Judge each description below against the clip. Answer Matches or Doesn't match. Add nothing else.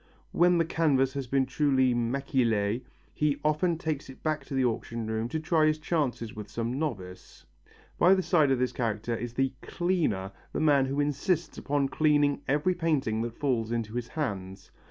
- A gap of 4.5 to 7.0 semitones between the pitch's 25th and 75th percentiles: Matches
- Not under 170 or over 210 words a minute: Matches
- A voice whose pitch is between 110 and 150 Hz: Matches